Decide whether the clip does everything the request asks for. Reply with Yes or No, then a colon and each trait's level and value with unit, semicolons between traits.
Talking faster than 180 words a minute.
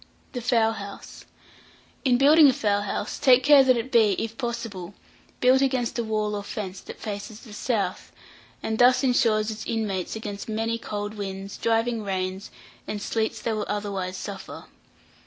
No: average, 165 wpm